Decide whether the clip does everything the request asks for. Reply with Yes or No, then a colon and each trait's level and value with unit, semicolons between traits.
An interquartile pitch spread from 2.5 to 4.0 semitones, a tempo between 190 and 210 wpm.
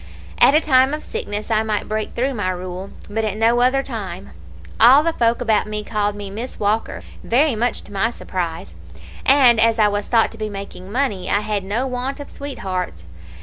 Yes: average, 3.5 semitones; average, 200 wpm